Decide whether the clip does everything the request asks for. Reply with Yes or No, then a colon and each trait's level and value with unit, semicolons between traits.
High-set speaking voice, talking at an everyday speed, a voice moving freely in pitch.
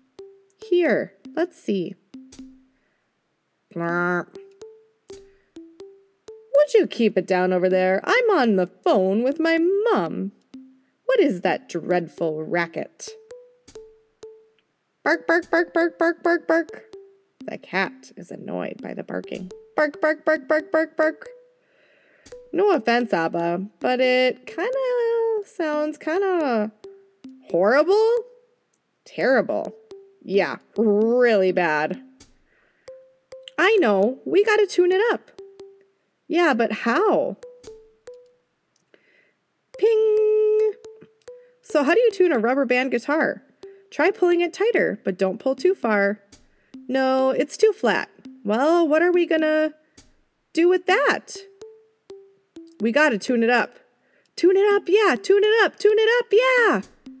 No: very high, 345 Hz; slow, 120 wpm; wide, 8.6 semitones